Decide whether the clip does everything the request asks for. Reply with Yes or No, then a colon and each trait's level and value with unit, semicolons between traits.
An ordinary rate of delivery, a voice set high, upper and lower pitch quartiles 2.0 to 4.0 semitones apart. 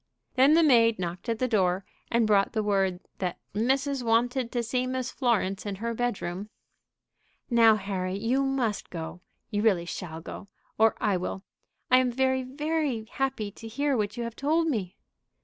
No: average, 170 wpm; high, 230 Hz; average, 4.6 semitones